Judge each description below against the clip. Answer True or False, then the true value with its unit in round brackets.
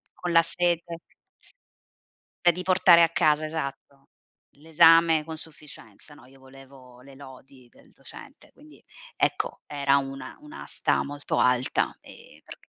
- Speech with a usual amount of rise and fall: True (3.6 semitones)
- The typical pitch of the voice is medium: True (150 Hz)